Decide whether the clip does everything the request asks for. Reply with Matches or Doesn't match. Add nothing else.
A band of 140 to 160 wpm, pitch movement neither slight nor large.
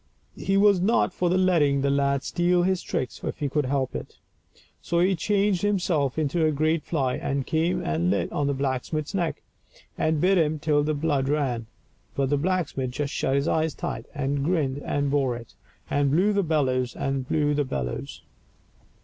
Doesn't match